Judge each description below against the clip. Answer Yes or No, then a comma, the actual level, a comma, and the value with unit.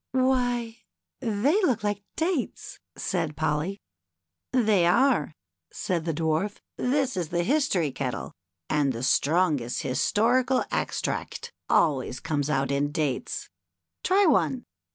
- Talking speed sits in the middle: No, slow, 130 wpm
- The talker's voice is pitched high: No, medium, 180 Hz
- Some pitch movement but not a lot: No, wide, 8.8 semitones